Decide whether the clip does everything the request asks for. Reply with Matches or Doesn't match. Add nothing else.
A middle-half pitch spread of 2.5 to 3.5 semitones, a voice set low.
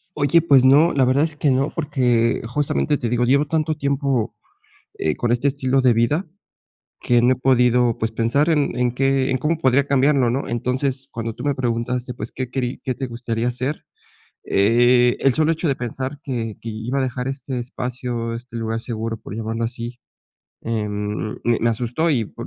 Matches